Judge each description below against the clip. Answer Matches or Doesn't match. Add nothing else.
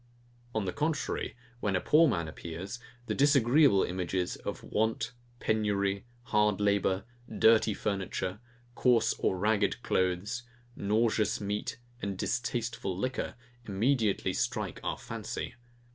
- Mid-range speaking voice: Doesn't match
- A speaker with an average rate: Doesn't match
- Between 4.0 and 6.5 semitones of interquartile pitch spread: Doesn't match